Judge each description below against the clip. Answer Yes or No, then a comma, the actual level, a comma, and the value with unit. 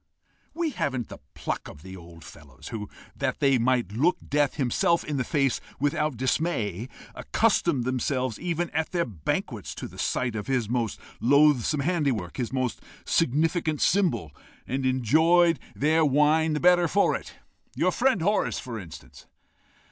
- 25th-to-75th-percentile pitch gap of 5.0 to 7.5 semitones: Yes, wide, 5.4 semitones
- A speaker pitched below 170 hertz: Yes, low, 135 Hz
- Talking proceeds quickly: No, average, 155 wpm